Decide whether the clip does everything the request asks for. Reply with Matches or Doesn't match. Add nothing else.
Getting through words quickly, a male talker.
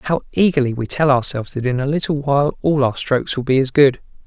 Matches